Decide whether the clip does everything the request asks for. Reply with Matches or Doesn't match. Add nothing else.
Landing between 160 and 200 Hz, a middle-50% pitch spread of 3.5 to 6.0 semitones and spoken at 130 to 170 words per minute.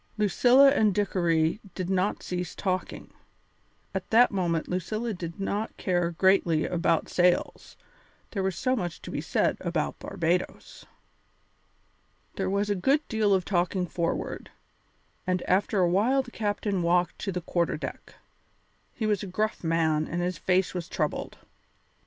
Doesn't match